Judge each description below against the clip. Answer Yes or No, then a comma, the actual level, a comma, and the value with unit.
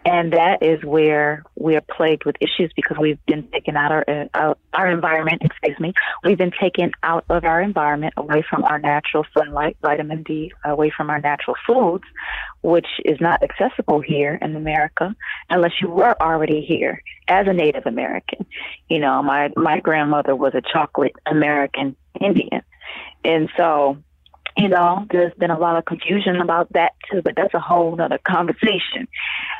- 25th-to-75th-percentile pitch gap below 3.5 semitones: Yes, narrow, 2.4 semitones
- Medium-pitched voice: Yes, medium, 155 Hz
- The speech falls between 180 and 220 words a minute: No, average, 170 wpm